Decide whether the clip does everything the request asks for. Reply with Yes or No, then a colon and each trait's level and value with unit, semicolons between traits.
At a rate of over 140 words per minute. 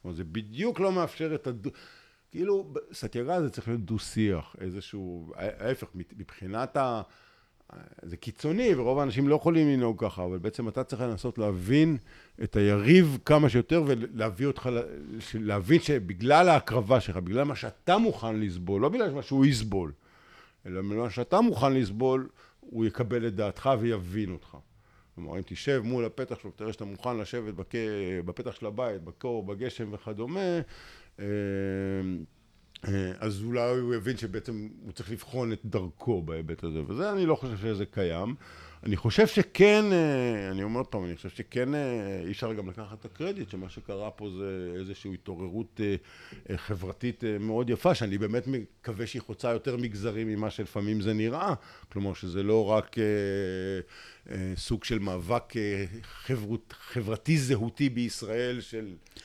Yes: fast, 150 wpm